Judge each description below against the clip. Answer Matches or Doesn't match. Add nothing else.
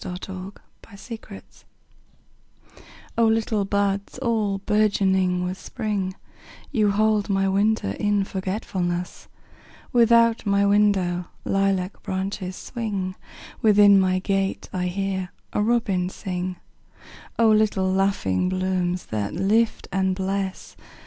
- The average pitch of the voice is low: Doesn't match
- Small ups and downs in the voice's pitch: Matches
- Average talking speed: Doesn't match